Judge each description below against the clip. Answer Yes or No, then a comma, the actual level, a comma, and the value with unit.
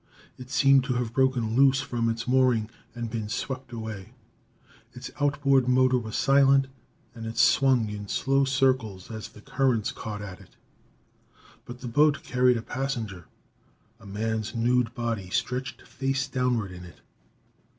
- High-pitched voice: No, low, 125 Hz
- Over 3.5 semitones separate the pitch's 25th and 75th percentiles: No, average, 3.1 semitones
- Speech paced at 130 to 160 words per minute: Yes, average, 150 wpm